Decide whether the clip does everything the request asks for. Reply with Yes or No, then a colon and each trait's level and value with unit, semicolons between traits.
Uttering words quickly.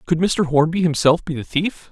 Yes: fast, 220 wpm